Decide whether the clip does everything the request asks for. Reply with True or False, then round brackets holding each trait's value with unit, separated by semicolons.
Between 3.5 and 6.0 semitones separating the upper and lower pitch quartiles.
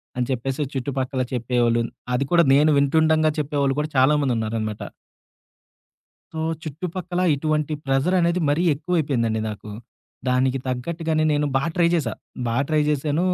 True (3.8 semitones)